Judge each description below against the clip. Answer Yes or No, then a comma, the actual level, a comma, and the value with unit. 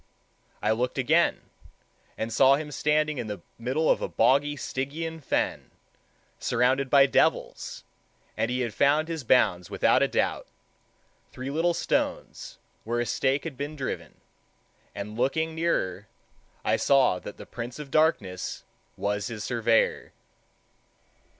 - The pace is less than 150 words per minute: Yes, slow, 135 wpm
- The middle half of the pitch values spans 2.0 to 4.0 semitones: No, average, 4.7 semitones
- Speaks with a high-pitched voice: No, low, 130 Hz